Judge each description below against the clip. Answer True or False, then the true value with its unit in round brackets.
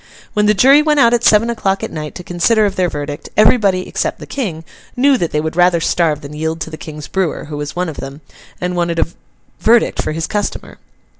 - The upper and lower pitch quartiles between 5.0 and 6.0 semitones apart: True (5.3 semitones)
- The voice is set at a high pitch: False (175 Hz)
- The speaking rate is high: True (230 wpm)